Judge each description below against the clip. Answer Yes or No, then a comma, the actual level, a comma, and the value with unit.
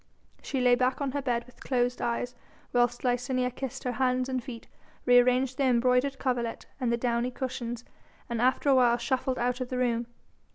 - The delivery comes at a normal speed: Yes, average, 195 wpm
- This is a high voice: Yes, very high, 250 Hz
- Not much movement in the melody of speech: Yes, narrow, 1.1 semitones